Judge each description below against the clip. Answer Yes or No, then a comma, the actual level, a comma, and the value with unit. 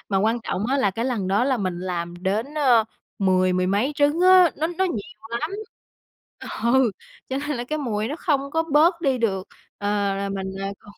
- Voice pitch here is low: No, high, 235 Hz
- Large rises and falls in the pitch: Yes, wide, 6.9 semitones